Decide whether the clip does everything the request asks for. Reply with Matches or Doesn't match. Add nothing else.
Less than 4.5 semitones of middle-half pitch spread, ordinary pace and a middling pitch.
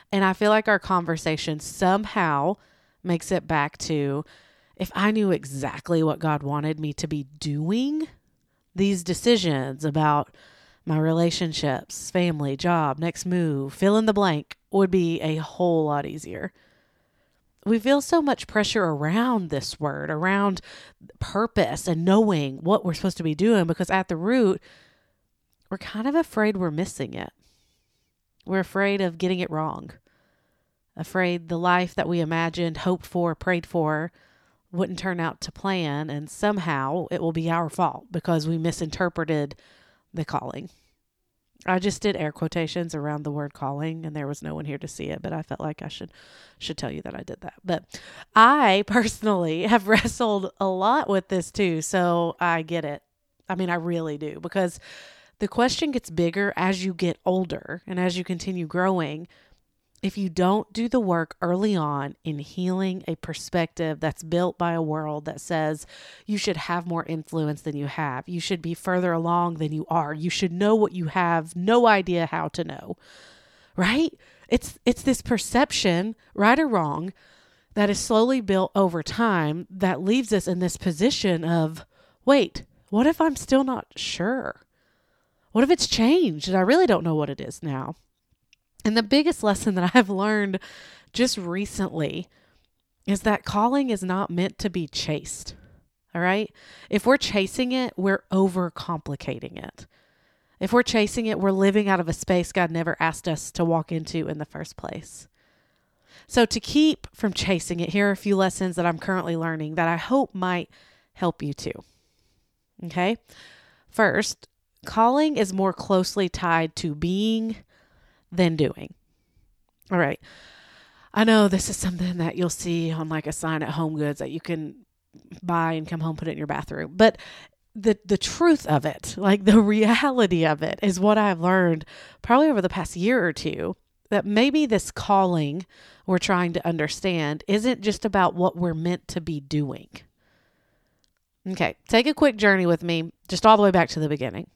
Matches